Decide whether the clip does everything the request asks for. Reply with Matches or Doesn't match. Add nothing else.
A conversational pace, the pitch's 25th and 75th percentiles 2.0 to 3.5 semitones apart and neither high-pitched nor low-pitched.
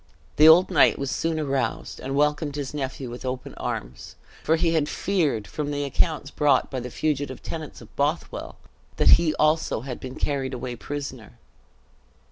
Matches